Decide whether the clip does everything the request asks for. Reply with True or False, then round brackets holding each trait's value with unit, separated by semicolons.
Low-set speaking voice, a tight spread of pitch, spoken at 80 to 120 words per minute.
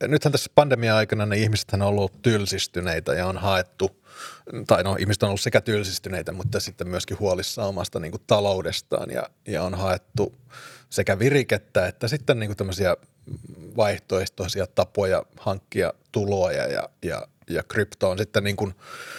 False (100 Hz; 2.2 semitones; 145 wpm)